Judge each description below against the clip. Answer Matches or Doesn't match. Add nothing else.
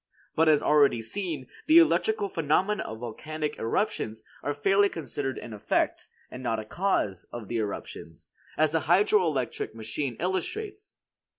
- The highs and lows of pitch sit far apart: Matches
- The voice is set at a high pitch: Doesn't match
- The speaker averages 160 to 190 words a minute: Doesn't match